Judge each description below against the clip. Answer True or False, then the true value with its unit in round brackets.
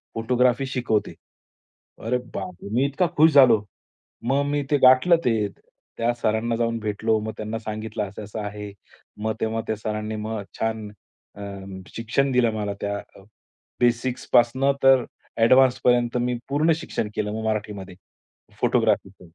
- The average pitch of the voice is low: True (115 Hz)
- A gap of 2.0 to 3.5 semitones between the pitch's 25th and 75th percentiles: True (2.9 semitones)